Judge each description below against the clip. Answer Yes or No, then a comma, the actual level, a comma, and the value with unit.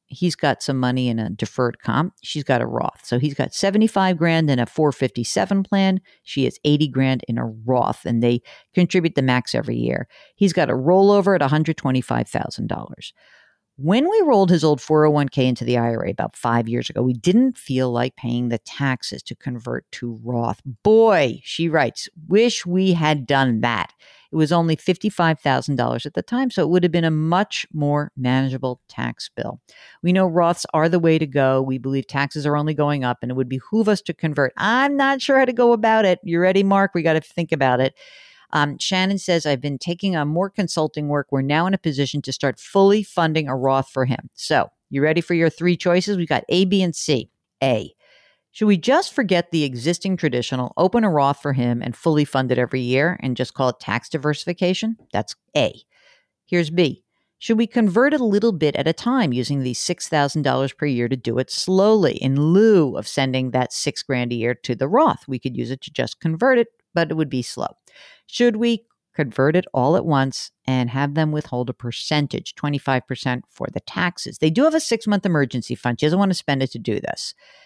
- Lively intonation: Yes, wide, 5.9 semitones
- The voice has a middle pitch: Yes, medium, 150 Hz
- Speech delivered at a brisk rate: Yes, fast, 210 wpm